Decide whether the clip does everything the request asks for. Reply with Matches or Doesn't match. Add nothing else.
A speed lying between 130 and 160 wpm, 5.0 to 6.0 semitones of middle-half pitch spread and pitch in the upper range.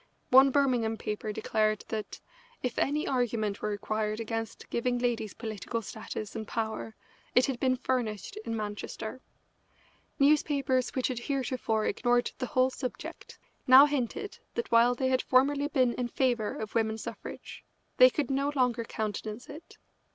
Doesn't match